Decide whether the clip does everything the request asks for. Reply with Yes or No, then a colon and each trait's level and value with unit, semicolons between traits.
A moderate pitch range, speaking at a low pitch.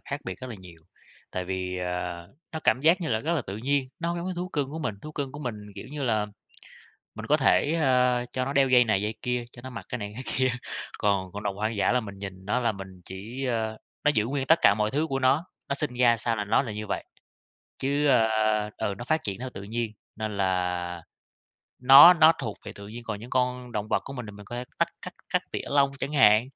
Yes: average, 4.9 semitones; low, 120 Hz